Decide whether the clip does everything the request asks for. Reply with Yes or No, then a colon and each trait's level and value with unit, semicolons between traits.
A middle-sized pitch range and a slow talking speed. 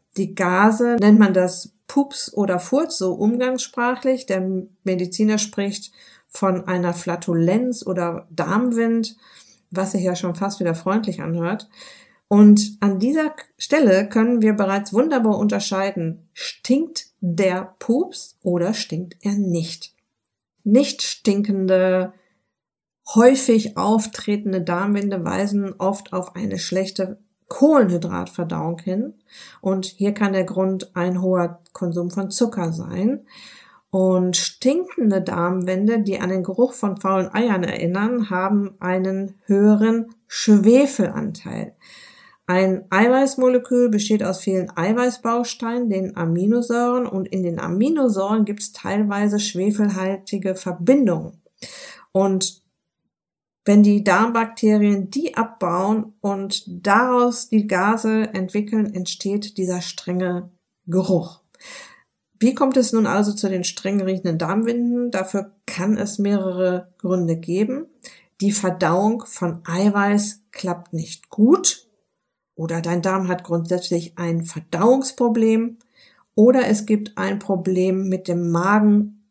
Yes: average, 3.5 semitones; slow, 115 wpm